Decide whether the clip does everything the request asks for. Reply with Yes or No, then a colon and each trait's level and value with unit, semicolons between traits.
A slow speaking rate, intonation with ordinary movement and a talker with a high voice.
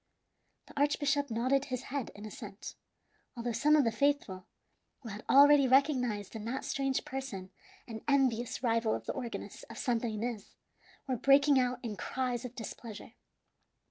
No: average, 155 wpm; average, 3.5 semitones; very high, 250 Hz